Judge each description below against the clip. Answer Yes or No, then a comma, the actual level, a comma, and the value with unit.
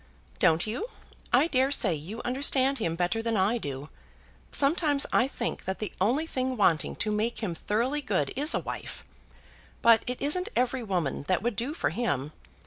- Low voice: No, high, 230 Hz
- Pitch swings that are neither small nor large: No, wide, 6.1 semitones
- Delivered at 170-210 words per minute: Yes, average, 180 wpm